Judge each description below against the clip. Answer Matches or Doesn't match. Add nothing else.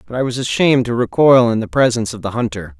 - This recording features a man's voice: Matches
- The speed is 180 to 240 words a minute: Doesn't match